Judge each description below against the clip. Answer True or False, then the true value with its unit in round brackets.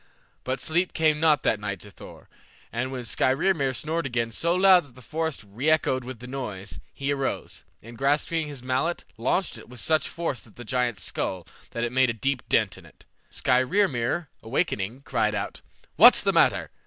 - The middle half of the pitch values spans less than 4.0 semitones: False (4.9 semitones)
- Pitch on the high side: False (130 Hz)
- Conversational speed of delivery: True (185 wpm)